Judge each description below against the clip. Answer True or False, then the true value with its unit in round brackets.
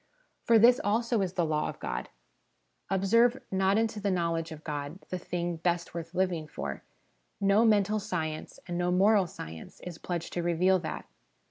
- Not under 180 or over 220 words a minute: False (170 wpm)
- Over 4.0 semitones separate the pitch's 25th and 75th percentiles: False (3.5 semitones)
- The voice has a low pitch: False (180 Hz)